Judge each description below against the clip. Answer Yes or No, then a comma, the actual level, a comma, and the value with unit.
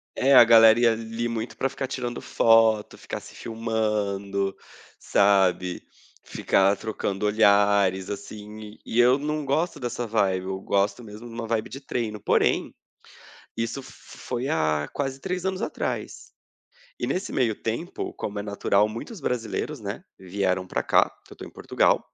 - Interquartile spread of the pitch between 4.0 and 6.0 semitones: No, average, 3.3 semitones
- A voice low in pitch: Yes, low, 110 Hz